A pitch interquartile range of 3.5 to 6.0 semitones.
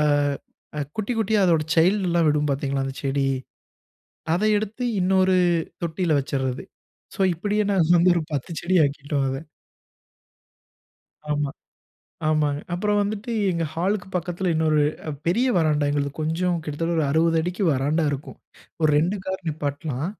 Yes: average, 4.2 semitones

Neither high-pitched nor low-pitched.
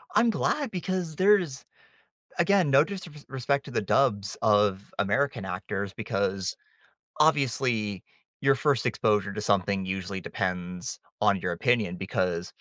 No: low, 105 Hz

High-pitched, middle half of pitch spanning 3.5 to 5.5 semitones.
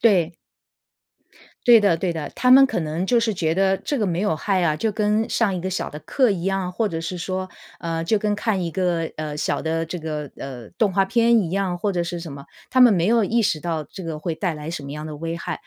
No: medium, 180 Hz; average, 4.1 semitones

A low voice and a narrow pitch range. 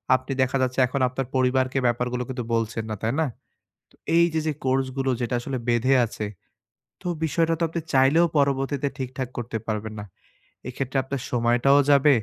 Yes: low, 130 Hz; narrow, 2.3 semitones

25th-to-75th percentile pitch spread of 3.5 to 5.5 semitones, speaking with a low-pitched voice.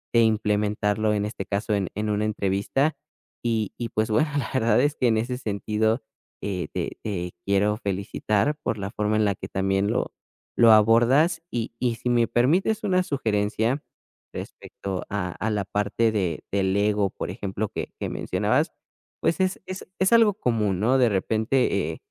No: average, 3.1 semitones; low, 110 Hz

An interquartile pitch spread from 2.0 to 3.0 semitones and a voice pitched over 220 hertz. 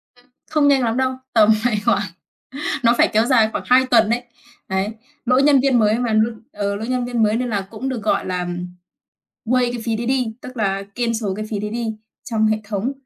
Yes: average, 2.7 semitones; high, 230 Hz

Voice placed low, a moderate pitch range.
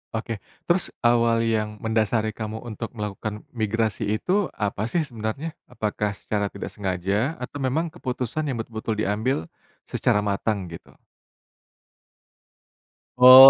Yes: low, 110 Hz; average, 3.1 semitones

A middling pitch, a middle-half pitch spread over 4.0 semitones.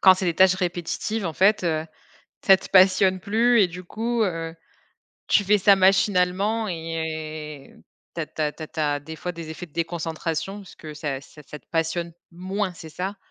No: medium, 175 Hz; average, 3.2 semitones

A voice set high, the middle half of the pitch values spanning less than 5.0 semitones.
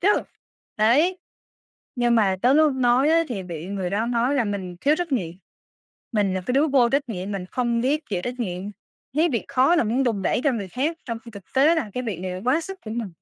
No: high, 240 Hz; wide, 5.6 semitones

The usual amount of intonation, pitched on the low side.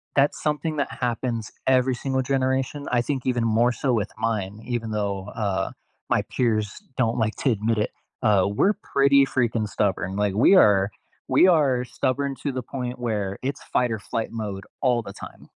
Yes: average, 3.7 semitones; low, 120 Hz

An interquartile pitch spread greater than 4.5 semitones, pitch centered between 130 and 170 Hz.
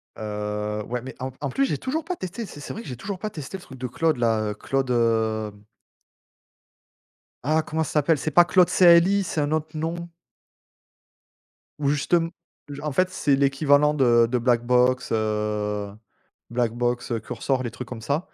Yes: wide, 5.5 semitones; low, 135 Hz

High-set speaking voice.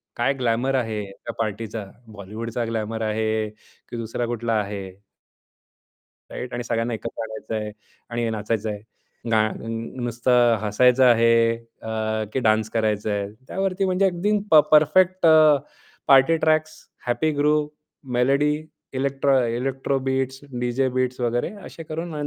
No: low, 120 Hz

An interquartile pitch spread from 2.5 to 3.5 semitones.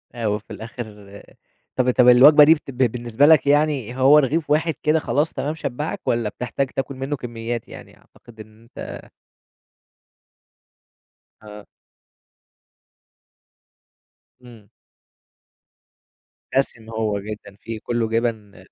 No: average, 4.2 semitones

